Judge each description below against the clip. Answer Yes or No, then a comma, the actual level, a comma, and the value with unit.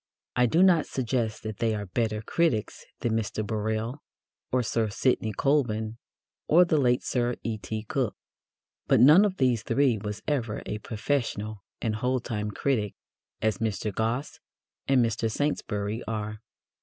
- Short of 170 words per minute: Yes, average, 150 wpm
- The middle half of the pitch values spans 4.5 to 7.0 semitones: No, average, 3.1 semitones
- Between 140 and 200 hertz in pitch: No, low, 115 Hz